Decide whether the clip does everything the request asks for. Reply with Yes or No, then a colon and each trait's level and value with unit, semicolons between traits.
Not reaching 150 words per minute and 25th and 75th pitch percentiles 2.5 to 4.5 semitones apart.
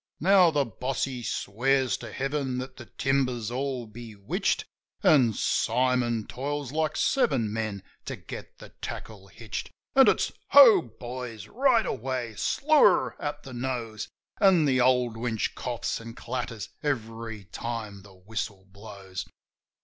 Yes: average, 140 wpm; average, 3.7 semitones